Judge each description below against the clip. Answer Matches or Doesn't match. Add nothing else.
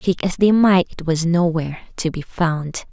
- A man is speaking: Doesn't match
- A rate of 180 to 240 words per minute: Matches